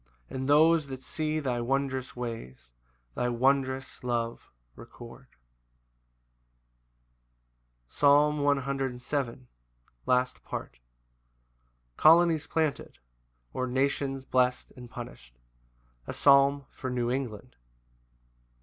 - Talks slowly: Yes, slow, 85 wpm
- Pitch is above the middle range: No, low, 130 Hz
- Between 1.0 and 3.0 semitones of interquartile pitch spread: Yes, narrow, 2.4 semitones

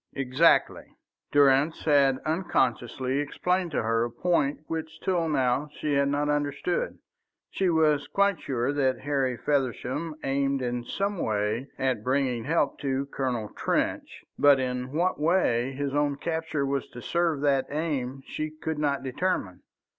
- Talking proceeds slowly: No, average, 145 wpm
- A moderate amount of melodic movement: Yes, average, 3.2 semitones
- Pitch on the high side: No, medium, 140 Hz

